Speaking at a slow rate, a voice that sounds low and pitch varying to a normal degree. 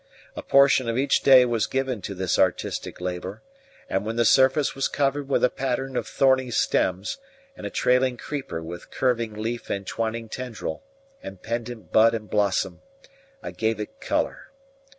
No: average, 170 wpm; low, 115 Hz; average, 4.0 semitones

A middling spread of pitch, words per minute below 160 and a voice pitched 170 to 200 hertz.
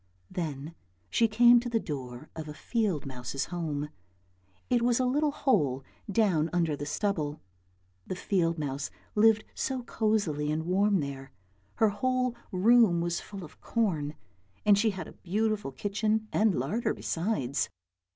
No: wide, 6.8 semitones; average, 150 wpm; medium, 185 Hz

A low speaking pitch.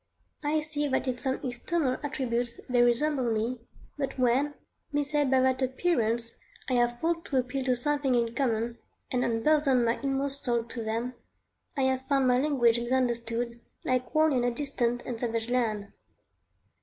No: very high, 255 Hz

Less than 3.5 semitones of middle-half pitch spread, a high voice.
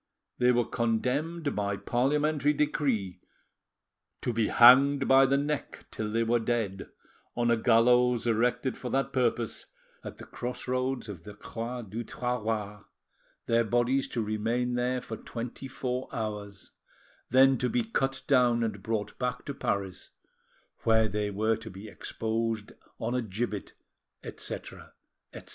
No: average, 2.7 semitones; low, 120 Hz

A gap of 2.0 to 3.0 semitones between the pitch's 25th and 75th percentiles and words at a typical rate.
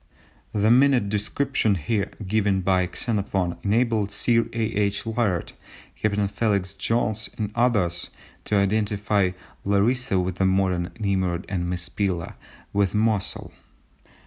No: narrow, 2.6 semitones; slow, 120 wpm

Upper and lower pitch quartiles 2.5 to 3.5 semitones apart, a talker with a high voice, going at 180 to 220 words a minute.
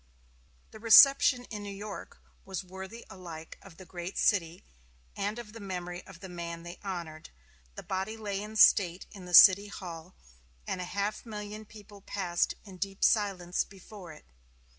No: average, 2.8 semitones; high, 195 Hz; average, 165 wpm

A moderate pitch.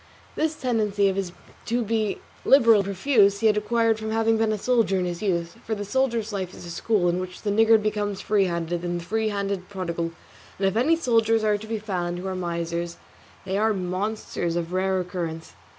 No: high, 200 Hz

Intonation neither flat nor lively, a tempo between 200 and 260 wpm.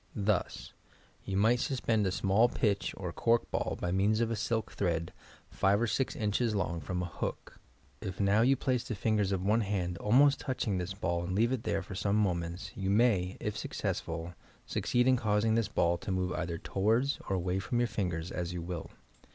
Yes: average, 4.0 semitones; fast, 205 wpm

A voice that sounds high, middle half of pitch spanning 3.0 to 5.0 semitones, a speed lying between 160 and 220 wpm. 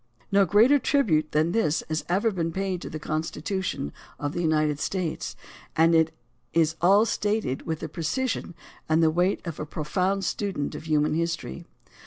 No: medium, 165 Hz; average, 3.9 semitones; average, 170 wpm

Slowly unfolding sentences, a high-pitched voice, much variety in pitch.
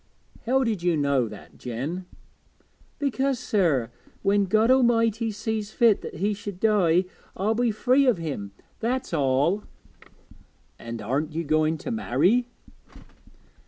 Yes: slow, 130 wpm; high, 200 Hz; wide, 6.9 semitones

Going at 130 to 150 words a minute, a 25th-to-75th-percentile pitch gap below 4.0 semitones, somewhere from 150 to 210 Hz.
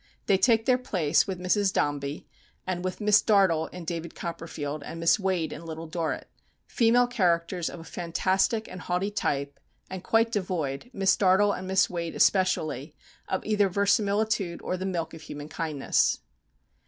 No: average, 165 wpm; average, 3.6 semitones; medium, 185 Hz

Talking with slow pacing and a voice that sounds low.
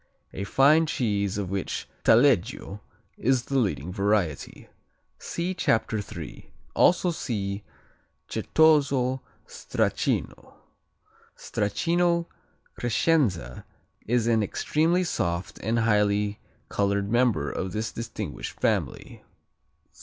Yes: slow, 95 wpm; low, 110 Hz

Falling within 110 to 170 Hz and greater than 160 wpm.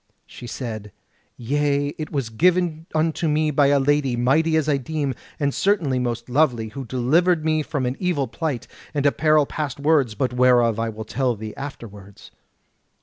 Yes: medium, 140 Hz; average, 175 wpm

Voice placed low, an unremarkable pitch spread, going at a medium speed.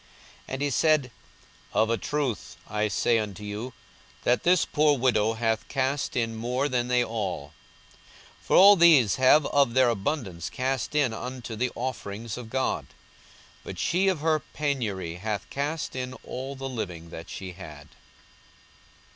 Yes: low, 125 Hz; average, 4.6 semitones; average, 160 wpm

